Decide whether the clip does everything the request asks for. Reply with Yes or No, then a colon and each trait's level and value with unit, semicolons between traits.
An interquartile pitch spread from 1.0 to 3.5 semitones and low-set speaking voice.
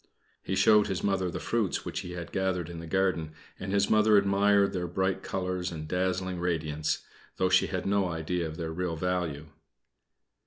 Yes: narrow, 2.5 semitones; very low, 90 Hz